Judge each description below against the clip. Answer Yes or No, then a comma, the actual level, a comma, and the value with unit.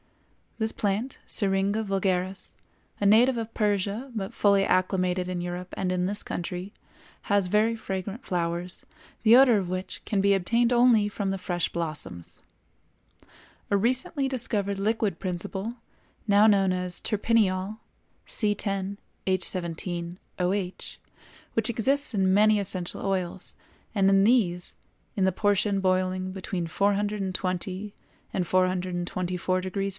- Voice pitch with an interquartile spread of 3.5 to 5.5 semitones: No, narrow, 2.4 semitones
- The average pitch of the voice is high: Yes, high, 195 Hz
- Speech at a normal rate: No, slow, 120 wpm